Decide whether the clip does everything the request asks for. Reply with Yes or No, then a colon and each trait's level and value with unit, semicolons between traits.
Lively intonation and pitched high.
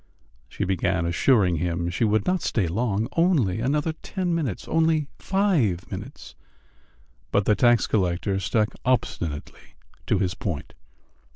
No: wide, 8.5 semitones; low, 105 Hz